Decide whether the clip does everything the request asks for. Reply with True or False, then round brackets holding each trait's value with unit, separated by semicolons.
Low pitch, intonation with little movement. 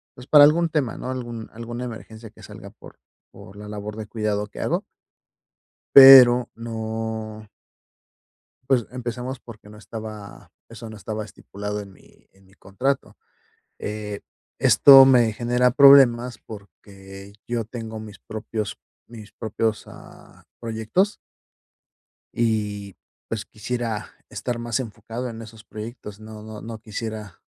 True (110 Hz; 2.3 semitones)